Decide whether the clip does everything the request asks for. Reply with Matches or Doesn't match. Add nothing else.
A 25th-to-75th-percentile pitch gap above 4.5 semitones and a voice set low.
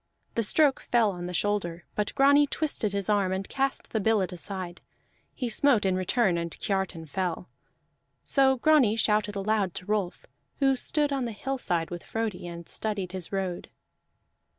Doesn't match